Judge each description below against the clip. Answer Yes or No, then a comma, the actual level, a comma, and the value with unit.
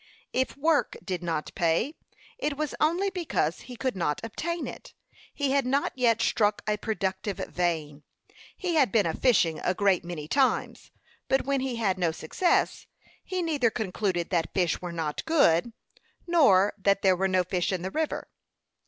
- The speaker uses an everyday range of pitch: No, wide, 7.7 semitones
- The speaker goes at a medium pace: Yes, average, 170 wpm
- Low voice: No, high, 205 Hz